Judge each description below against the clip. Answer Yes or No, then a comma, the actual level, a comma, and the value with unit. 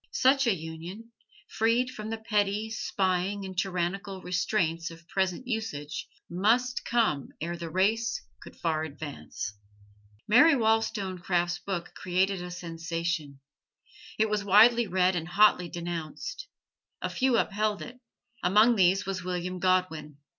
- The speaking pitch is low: No, high, 190 Hz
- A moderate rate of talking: No, slow, 130 wpm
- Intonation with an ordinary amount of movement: Yes, average, 4.2 semitones